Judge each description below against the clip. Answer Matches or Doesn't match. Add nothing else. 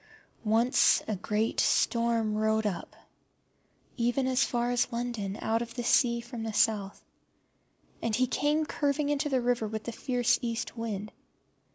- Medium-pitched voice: Doesn't match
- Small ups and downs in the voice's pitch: Matches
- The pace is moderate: Matches